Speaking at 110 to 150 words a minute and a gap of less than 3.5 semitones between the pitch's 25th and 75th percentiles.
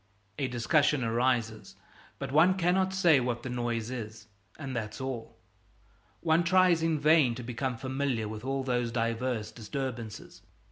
No: average, 145 wpm; average, 4.3 semitones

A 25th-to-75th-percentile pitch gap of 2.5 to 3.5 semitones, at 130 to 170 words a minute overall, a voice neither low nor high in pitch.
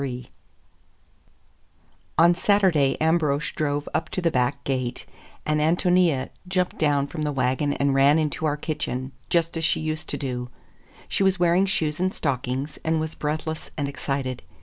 Yes: average, 3.0 semitones; average, 160 wpm; medium, 150 Hz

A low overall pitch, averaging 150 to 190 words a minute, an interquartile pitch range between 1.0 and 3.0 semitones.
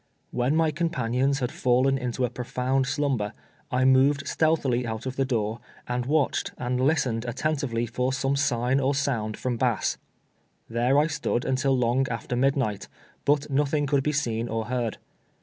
Yes: low, 130 Hz; average, 170 wpm; narrow, 2.5 semitones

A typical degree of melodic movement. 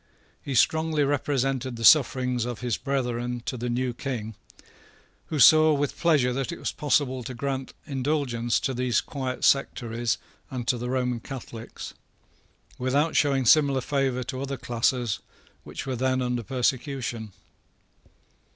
No: narrow, 2.2 semitones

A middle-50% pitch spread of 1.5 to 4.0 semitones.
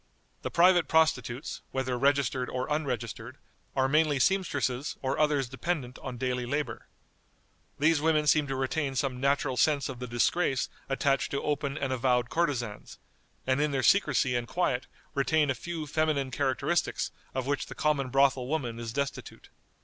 Yes: average, 3.0 semitones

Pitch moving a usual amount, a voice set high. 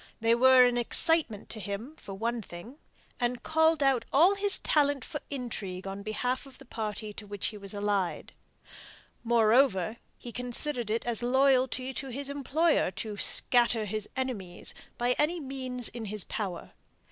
Yes: average, 4.2 semitones; high, 240 Hz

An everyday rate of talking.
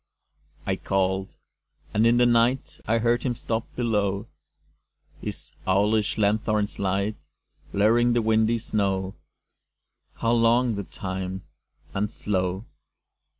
No: slow, 110 wpm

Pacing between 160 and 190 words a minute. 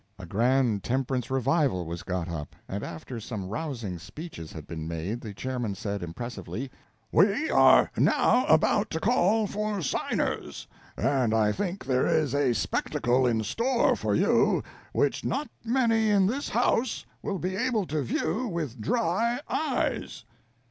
No: average, 150 wpm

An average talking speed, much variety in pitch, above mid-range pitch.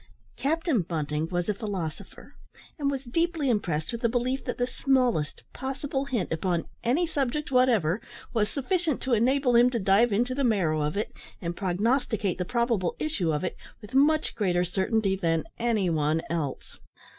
Yes: average, 170 wpm; wide, 6.9 semitones; high, 230 Hz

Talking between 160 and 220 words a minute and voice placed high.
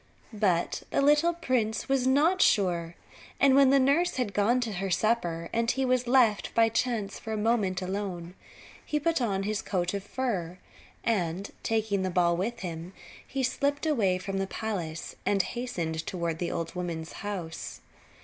Yes: average, 170 wpm; high, 205 Hz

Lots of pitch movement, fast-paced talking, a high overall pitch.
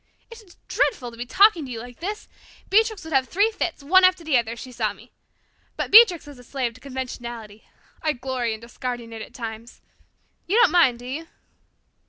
Yes: wide, 7.0 semitones; fast, 210 wpm; very high, 265 Hz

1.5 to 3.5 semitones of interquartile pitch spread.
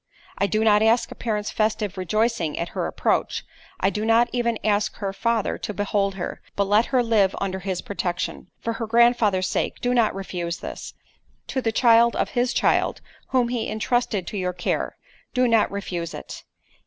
Yes: average, 3.2 semitones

